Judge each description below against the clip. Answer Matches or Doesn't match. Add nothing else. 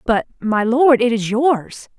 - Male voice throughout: Doesn't match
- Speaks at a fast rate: Doesn't match